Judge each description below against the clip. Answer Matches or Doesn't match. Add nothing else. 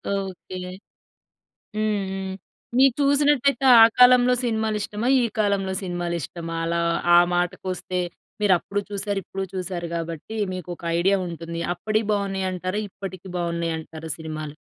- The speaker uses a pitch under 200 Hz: Matches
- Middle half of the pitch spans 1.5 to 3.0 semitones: Doesn't match